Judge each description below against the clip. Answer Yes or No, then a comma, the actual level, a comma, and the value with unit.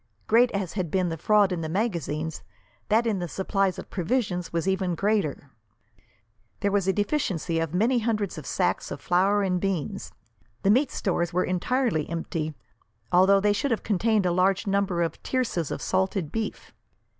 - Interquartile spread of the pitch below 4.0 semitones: Yes, average, 3.3 semitones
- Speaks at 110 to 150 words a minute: No, average, 175 wpm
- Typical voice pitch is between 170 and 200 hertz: Yes, high, 190 Hz